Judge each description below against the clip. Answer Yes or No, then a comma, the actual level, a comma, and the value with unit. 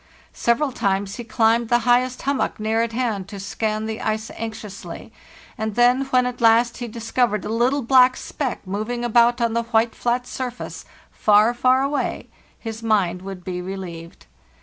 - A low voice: No, high, 230 Hz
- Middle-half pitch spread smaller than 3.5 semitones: Yes, narrow, 2.4 semitones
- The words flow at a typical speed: Yes, average, 170 wpm